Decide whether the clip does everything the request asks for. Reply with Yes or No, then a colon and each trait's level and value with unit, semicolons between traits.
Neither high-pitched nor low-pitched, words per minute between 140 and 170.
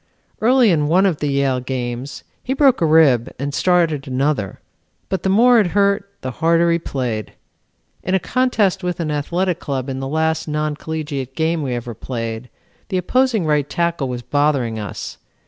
No: medium, 155 Hz; average, 180 wpm